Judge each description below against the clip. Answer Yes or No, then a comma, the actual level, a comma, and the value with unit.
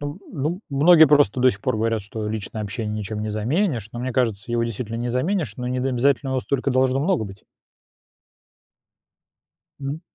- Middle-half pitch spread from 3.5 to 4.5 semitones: Yes, average, 4.2 semitones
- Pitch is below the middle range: Yes, low, 125 Hz